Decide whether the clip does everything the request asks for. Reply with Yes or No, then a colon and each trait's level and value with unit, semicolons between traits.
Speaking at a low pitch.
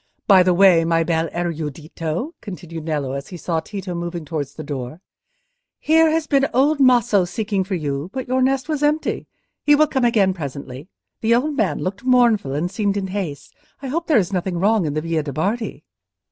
No: medium, 185 Hz